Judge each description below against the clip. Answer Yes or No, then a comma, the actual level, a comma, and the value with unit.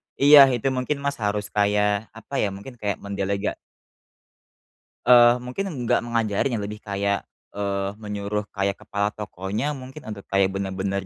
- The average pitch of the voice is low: Yes, low, 105 Hz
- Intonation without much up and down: No, average, 3.5 semitones